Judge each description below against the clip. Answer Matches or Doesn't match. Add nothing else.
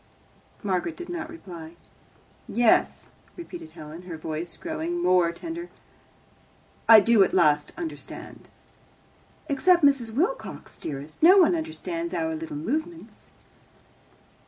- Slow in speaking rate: Matches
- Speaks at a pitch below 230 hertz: Doesn't match